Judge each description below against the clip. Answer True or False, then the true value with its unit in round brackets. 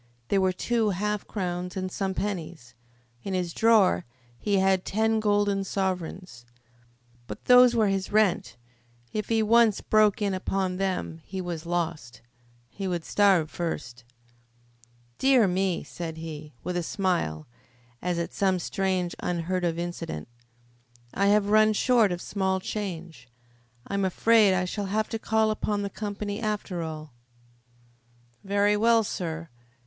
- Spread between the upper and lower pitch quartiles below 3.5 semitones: True (3.1 semitones)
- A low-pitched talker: False (190 Hz)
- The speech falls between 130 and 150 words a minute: True (145 wpm)